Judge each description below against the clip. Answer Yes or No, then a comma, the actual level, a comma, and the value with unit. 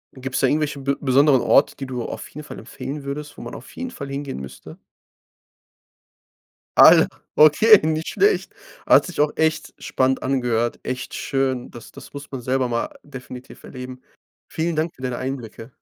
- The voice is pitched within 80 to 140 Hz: Yes, low, 135 Hz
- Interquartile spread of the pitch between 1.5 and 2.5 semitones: No, average, 2.9 semitones